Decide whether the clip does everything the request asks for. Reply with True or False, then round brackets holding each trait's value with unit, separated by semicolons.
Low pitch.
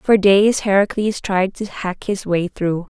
False (195 Hz)